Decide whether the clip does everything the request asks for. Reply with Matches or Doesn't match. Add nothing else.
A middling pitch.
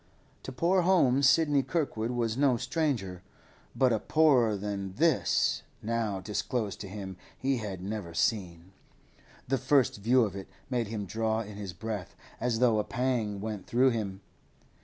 Doesn't match